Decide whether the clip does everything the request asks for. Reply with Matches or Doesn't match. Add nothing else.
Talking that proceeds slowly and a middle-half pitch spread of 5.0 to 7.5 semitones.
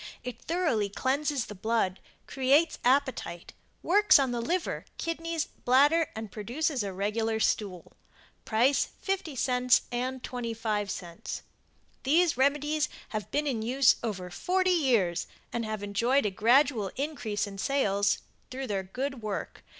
Matches